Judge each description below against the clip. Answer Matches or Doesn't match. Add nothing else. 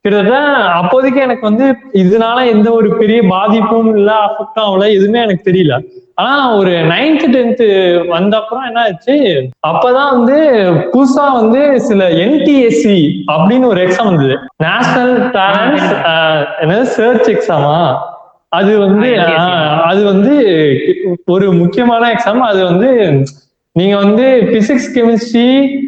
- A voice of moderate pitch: Doesn't match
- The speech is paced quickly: Doesn't match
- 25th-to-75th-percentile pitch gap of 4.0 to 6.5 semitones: Matches